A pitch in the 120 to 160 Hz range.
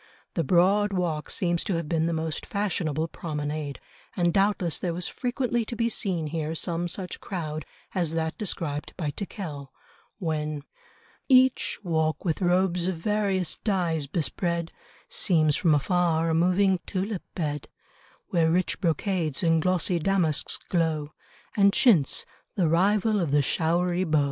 No: medium, 170 Hz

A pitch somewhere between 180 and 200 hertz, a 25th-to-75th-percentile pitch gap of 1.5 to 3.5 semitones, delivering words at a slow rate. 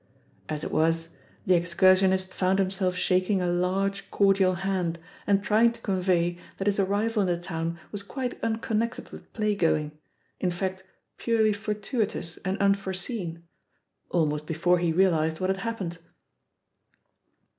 No: high, 190 Hz; narrow, 2.6 semitones; average, 145 wpm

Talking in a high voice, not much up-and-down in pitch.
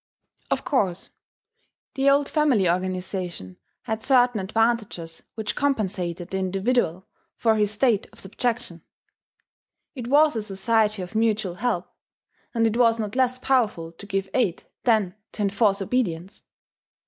No: high, 210 Hz; average, 4.4 semitones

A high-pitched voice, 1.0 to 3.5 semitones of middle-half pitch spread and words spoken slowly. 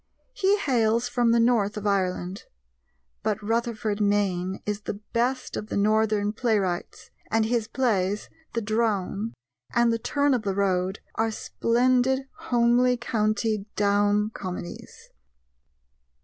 Yes: high, 220 Hz; average, 2.7 semitones; slow, 125 wpm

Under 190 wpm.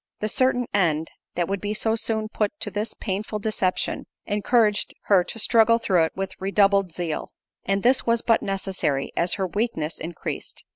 Yes: average, 175 wpm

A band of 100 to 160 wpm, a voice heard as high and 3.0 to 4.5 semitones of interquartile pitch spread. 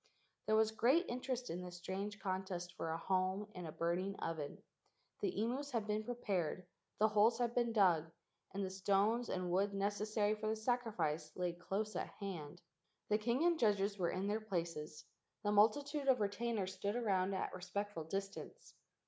No: average, 180 wpm; high, 200 Hz; average, 3.3 semitones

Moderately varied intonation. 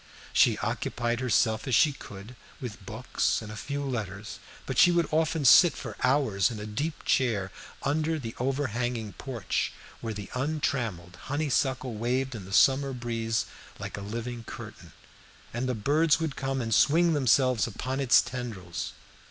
Yes: average, 3.9 semitones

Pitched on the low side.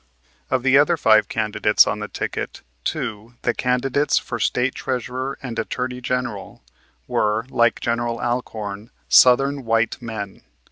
Yes: low, 120 Hz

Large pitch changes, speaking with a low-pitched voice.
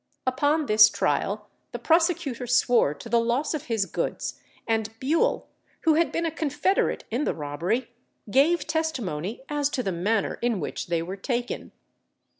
No: wide, 6.3 semitones; high, 245 Hz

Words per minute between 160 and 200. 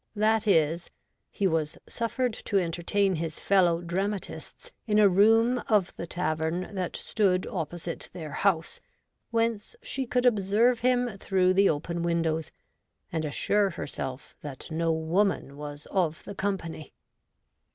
No: slow, 135 wpm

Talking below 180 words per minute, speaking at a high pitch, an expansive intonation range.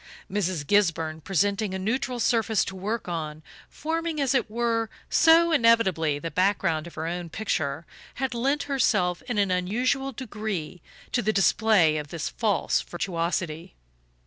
Yes: average, 145 wpm; high, 200 Hz; wide, 5.7 semitones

